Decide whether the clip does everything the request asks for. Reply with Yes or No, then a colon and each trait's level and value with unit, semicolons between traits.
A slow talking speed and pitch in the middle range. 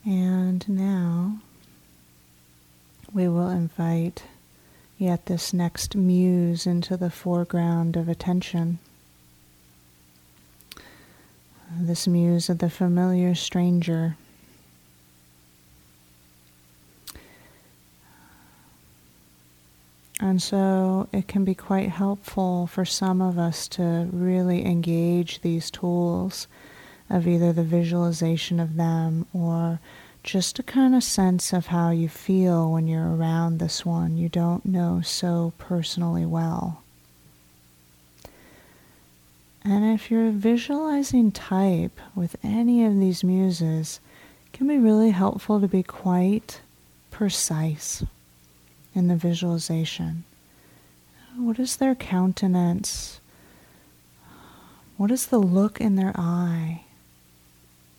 Yes: slow, 100 wpm; medium, 170 Hz